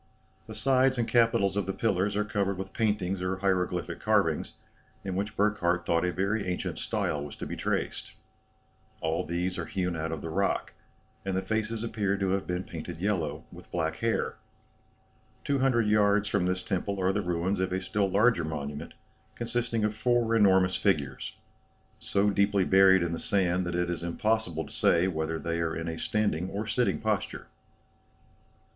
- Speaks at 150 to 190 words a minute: Yes, average, 180 wpm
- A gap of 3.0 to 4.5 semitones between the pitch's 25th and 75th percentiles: Yes, average, 3.3 semitones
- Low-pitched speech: Yes, very low, 95 Hz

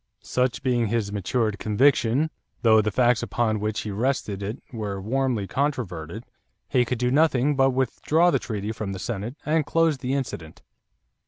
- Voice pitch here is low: Yes, low, 120 Hz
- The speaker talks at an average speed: Yes, average, 165 wpm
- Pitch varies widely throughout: No, average, 4.1 semitones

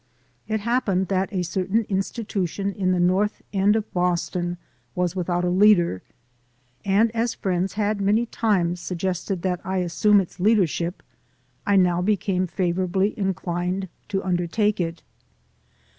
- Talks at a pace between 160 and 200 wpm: No, slow, 135 wpm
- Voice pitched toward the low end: No, high, 190 Hz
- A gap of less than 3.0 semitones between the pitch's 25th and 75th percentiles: Yes, narrow, 2.5 semitones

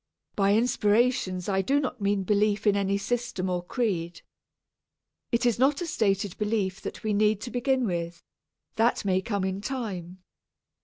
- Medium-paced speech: Yes, average, 160 wpm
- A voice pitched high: Yes, high, 205 Hz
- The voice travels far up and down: No, average, 4.0 semitones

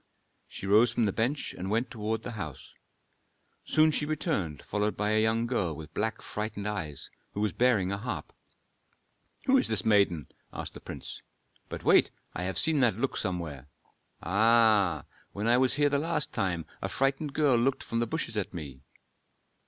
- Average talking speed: Yes, average, 180 wpm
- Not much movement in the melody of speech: No, average, 4.9 semitones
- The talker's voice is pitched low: Yes, low, 110 Hz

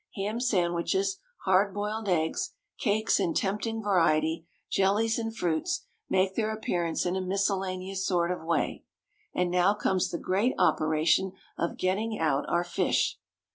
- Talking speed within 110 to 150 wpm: Yes, average, 140 wpm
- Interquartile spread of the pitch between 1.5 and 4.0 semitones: Yes, average, 3.5 semitones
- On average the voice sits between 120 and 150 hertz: No, high, 190 Hz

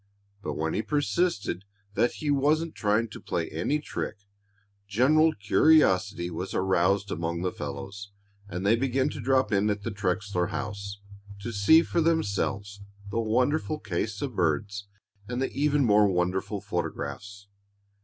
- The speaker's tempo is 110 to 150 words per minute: Yes, average, 145 wpm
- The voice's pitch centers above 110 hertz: No, low, 105 Hz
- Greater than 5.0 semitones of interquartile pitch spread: Yes, wide, 5.5 semitones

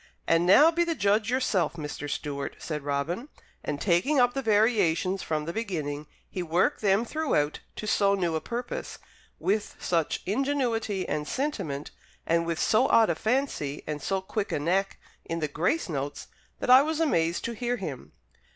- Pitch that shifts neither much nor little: No, wide, 7.1 semitones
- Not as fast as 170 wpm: No, average, 175 wpm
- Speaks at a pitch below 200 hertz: Yes, high, 190 Hz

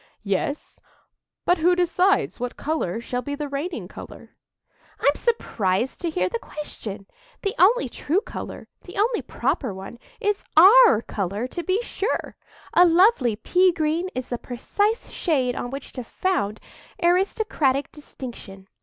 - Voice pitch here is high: Yes, very high, 300 Hz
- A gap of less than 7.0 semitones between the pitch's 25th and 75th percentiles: No, wide, 7.5 semitones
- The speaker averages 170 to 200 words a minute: No, slow, 135 wpm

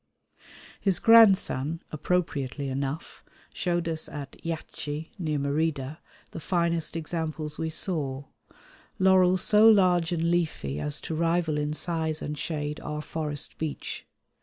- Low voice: No, medium, 160 Hz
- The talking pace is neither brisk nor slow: No, slow, 125 wpm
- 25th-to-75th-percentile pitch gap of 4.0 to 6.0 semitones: No, average, 2.7 semitones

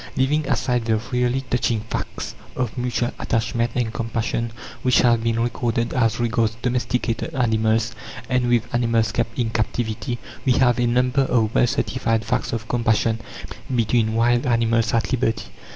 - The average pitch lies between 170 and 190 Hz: No, low, 115 Hz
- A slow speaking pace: No, average, 150 wpm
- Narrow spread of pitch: Yes, narrow, 1.5 semitones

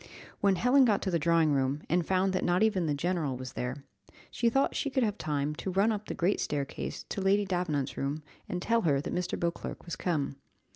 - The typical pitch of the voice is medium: Yes, medium, 175 Hz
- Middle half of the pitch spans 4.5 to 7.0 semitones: Yes, average, 5.3 semitones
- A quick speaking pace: Yes, fast, 225 wpm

